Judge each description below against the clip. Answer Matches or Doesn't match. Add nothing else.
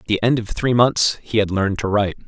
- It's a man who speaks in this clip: Matches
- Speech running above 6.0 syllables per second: Matches